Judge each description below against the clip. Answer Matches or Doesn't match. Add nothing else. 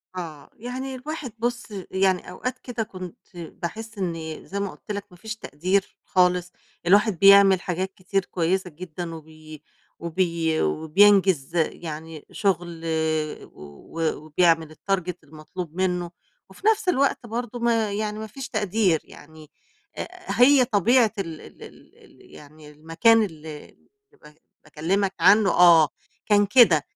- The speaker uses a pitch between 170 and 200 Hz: Matches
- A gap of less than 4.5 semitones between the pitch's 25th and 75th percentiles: Doesn't match